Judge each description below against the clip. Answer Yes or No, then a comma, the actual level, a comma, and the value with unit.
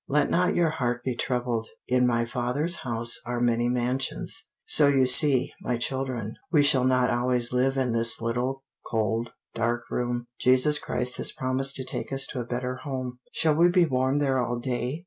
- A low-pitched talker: Yes, low, 125 Hz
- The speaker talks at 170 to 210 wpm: Yes, average, 185 wpm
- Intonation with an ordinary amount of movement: No, narrow, 1.9 semitones